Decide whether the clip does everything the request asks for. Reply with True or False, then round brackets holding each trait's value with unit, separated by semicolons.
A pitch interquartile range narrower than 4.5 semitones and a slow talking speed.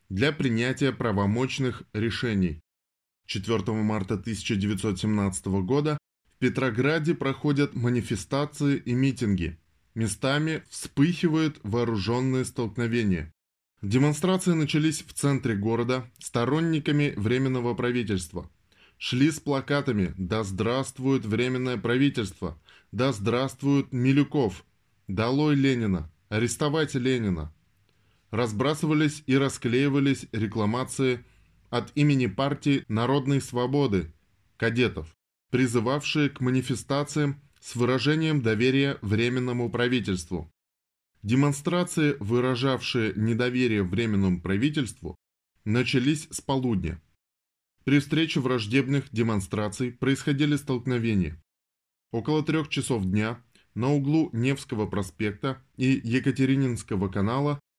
False (5.2 semitones; 85 wpm)